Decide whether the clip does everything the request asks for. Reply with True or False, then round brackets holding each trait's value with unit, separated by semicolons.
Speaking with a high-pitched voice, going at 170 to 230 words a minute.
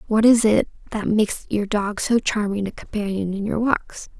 True (210 Hz; 200 wpm)